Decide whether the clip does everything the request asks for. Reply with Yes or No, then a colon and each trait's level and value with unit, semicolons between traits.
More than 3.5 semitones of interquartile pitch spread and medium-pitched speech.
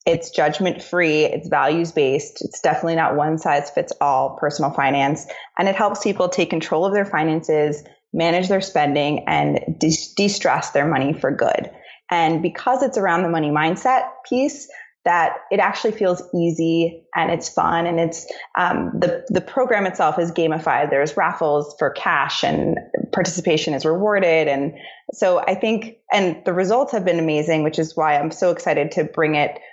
Yes: average, 4.1 semitones; medium, 165 Hz